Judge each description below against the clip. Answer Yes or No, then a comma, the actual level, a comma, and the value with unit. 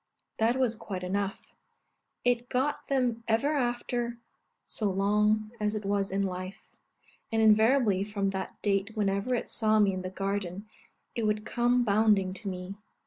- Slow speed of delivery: No, average, 155 wpm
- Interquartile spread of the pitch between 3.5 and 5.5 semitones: No, average, 3.1 semitones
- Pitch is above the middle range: Yes, high, 210 Hz